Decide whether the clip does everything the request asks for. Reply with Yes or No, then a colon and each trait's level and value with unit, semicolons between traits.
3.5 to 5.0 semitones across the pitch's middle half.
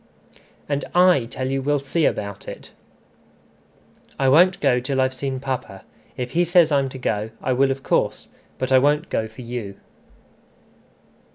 No: average, 2.7 semitones